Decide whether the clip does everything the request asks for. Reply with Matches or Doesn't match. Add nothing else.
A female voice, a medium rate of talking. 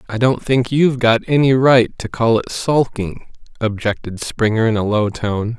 Doesn't match